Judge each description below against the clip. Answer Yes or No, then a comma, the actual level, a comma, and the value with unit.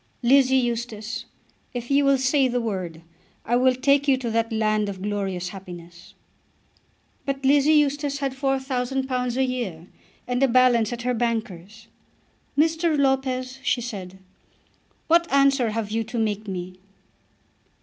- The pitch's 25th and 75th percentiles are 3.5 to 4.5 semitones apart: Yes, average, 4.0 semitones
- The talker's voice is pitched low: No, high, 245 Hz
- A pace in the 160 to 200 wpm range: No, average, 140 wpm